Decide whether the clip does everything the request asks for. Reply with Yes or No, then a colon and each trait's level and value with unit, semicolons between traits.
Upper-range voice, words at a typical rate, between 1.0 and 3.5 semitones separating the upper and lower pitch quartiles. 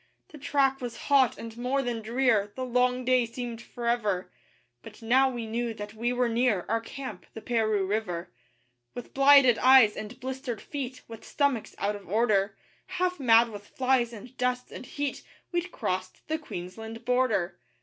Yes: high, 240 Hz; average, 170 wpm; average, 3.0 semitones